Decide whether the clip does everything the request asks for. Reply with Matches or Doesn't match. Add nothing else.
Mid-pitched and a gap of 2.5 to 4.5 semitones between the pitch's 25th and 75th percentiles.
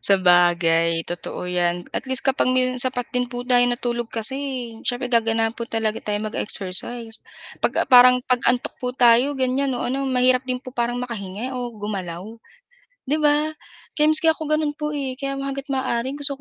Doesn't match